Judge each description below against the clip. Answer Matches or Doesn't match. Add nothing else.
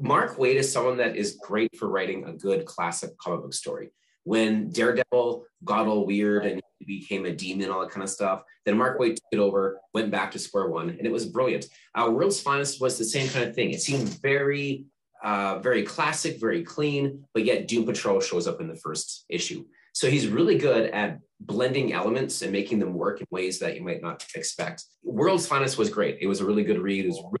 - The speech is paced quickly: Matches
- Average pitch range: Doesn't match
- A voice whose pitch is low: Matches